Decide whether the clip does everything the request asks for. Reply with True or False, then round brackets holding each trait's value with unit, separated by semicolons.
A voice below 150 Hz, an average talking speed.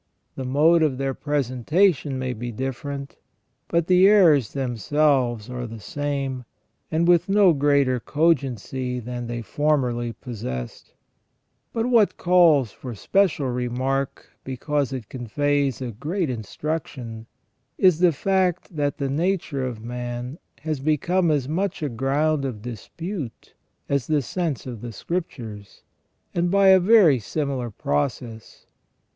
False (140 Hz; 130 wpm)